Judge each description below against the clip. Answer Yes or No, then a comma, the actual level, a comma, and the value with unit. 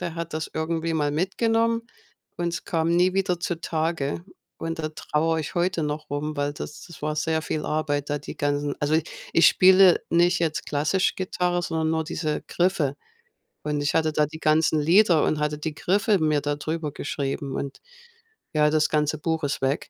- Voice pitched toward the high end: No, medium, 160 Hz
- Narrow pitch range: Yes, narrow, 2.3 semitones